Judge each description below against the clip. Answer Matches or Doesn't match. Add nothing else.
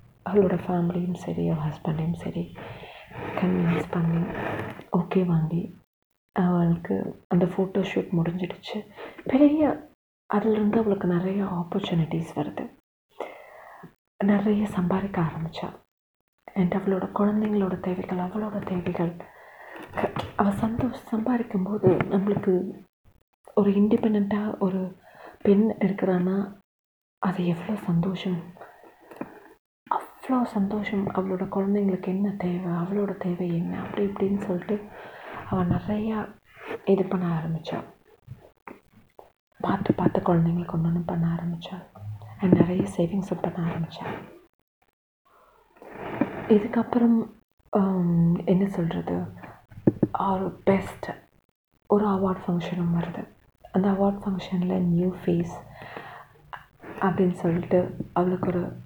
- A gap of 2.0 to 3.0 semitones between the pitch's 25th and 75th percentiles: Matches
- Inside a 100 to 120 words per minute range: Doesn't match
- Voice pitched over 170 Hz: Matches